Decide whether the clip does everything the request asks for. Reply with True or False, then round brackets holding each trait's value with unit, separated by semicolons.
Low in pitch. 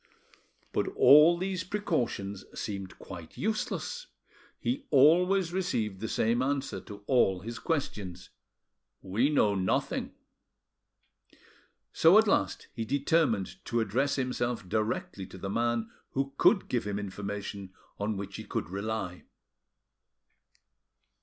True (115 Hz)